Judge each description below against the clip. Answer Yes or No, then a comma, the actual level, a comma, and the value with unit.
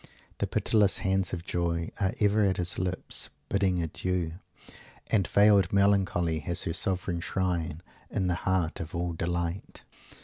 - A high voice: No, very low, 90 Hz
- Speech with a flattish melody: Yes, narrow, 2.2 semitones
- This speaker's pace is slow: No, average, 145 wpm